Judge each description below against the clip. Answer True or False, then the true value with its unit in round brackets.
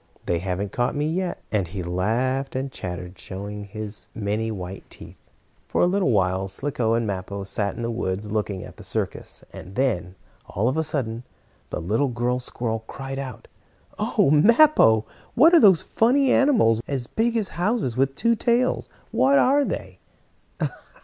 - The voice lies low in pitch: True (120 Hz)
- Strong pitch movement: True (7.8 semitones)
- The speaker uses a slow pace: False (170 wpm)